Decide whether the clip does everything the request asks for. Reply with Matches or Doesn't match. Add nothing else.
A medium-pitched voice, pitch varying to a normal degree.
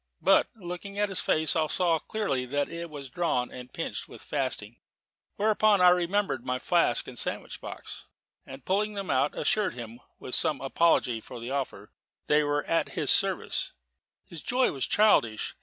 Doesn't match